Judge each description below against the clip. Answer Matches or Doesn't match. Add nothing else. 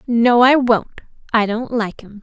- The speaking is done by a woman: Matches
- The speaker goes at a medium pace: Matches